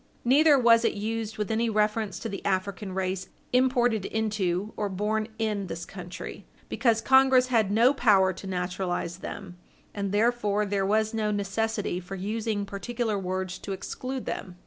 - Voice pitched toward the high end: Yes, high, 210 Hz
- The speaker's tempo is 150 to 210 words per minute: Yes, average, 160 wpm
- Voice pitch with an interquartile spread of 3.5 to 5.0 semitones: No, average, 2.9 semitones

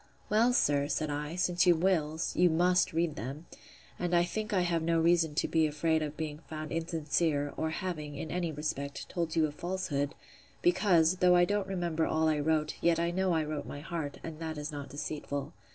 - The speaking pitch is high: No, medium, 160 Hz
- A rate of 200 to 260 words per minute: Yes, fast, 205 wpm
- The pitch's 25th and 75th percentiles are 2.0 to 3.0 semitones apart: Yes, average, 2.7 semitones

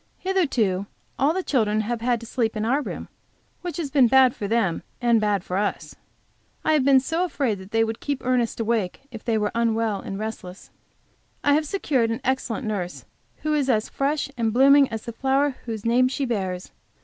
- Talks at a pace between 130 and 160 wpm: No, average, 195 wpm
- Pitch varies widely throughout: No, average, 4.1 semitones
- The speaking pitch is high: Yes, high, 235 Hz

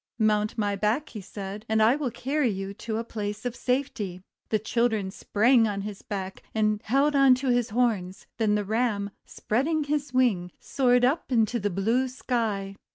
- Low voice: No, high, 220 Hz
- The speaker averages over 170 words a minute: Yes, average, 180 wpm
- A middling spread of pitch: Yes, average, 3.5 semitones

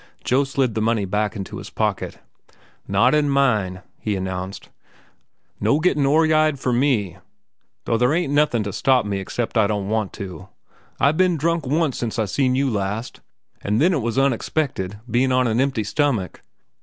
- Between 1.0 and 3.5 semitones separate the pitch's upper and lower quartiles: No, wide, 5.4 semitones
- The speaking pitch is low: Yes, low, 120 Hz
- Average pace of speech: Yes, average, 175 wpm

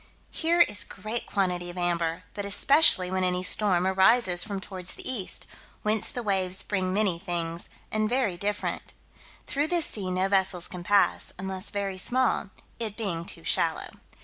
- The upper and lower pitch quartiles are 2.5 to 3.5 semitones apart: Yes, average, 2.9 semitones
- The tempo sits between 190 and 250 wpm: No, average, 165 wpm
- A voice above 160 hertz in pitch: Yes, high, 190 Hz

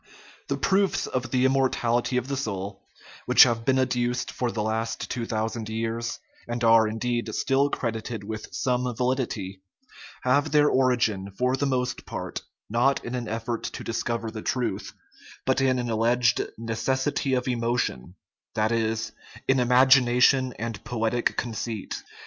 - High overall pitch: No, low, 120 Hz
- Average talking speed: Yes, average, 155 wpm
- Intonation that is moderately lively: No, narrow, 2.2 semitones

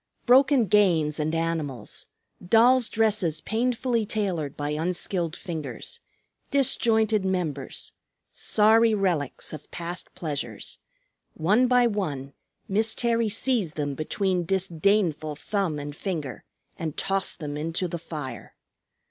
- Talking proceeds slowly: Yes, slow, 115 wpm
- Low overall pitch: No, medium, 180 Hz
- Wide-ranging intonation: Yes, wide, 5.9 semitones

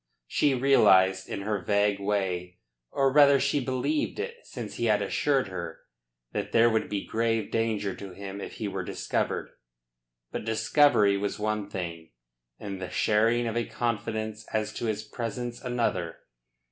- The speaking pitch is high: No, low, 110 Hz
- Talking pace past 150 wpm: Yes, average, 160 wpm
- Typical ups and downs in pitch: Yes, average, 3.3 semitones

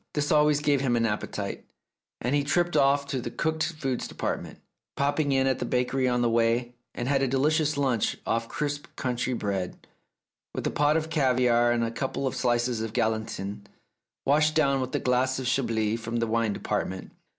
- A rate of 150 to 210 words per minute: Yes, average, 190 wpm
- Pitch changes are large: No, average, 3.5 semitones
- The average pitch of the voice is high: No, low, 130 Hz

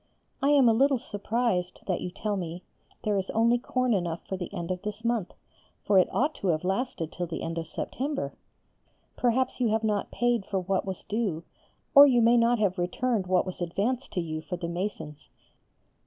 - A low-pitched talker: No, high, 205 Hz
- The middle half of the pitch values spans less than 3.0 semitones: No, average, 5.1 semitones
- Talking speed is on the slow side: No, average, 200 wpm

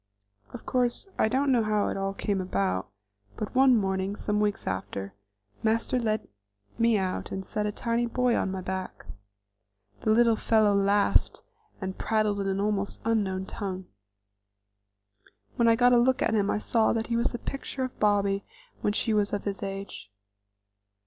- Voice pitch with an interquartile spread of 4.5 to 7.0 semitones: No, average, 2.9 semitones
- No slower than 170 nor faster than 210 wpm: Yes, average, 175 wpm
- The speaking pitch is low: No, high, 210 Hz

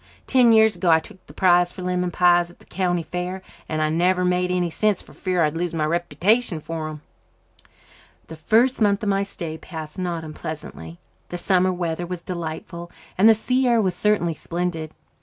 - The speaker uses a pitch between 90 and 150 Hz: No, medium, 180 Hz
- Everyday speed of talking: Yes, average, 195 wpm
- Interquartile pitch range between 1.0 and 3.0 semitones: Yes, narrow, 2.4 semitones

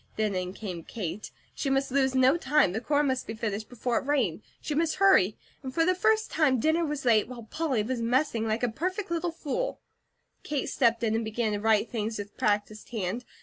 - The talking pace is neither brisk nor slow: No, fast, 210 wpm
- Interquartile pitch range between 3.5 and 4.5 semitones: No, wide, 5.5 semitones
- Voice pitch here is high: Yes, high, 245 Hz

